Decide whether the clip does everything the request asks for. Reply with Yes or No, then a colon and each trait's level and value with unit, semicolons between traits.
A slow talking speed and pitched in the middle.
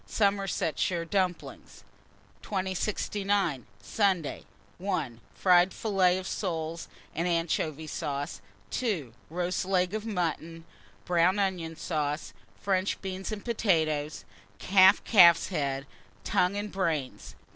Yes: slow, 100 wpm; medium, 180 Hz